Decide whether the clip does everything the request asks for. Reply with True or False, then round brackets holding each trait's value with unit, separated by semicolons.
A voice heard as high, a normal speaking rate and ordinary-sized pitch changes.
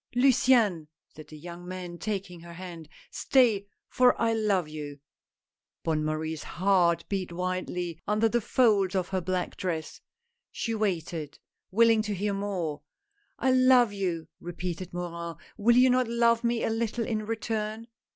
True (195 Hz; 160 wpm; 4.8 semitones)